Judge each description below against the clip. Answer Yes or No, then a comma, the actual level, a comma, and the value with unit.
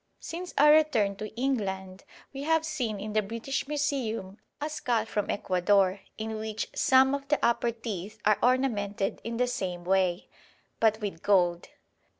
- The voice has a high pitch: Yes, high, 220 Hz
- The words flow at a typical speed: Yes, average, 155 wpm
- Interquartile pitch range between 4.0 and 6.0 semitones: Yes, average, 5.2 semitones